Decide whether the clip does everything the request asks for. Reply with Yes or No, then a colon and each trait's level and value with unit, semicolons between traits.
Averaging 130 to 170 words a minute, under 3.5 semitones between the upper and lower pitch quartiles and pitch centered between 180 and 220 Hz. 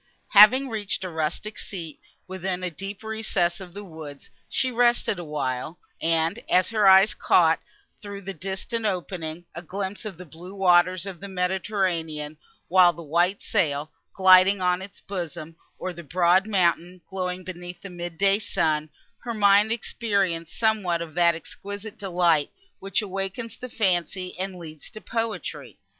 Yes: average, 155 wpm; average, 2.8 semitones; medium, 185 Hz